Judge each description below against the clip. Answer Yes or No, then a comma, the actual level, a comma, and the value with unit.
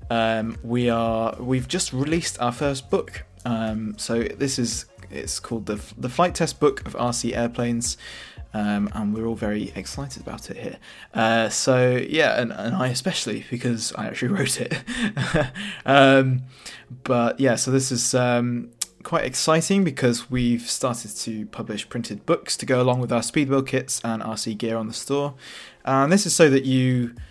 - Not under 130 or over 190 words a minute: Yes, average, 175 wpm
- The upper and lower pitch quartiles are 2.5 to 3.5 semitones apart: Yes, average, 2.9 semitones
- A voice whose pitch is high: No, low, 120 Hz